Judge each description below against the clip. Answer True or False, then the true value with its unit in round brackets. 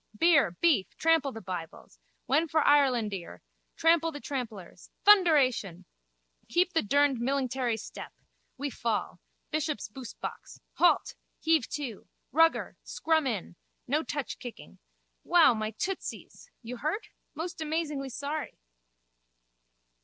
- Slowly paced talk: True (115 wpm)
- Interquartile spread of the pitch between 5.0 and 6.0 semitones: True (5.6 semitones)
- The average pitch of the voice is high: True (280 Hz)